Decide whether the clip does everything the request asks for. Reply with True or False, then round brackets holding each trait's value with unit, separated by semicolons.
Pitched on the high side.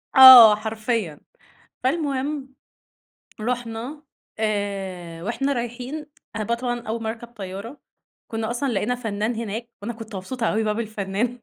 True (230 Hz)